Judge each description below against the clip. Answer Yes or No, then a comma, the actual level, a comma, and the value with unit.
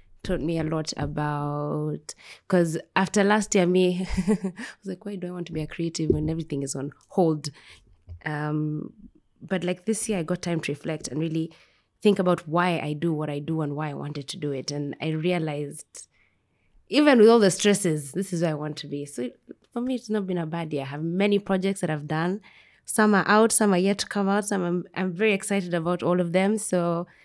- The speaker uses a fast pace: Yes, fast, 225 wpm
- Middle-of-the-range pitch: Yes, medium, 175 Hz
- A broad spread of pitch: No, average, 4.3 semitones